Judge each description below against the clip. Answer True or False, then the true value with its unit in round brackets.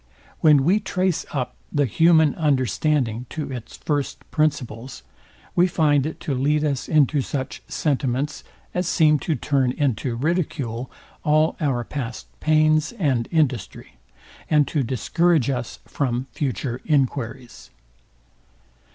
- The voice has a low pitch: False (145 Hz)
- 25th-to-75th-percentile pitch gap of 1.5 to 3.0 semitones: False (3.5 semitones)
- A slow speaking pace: True (125 wpm)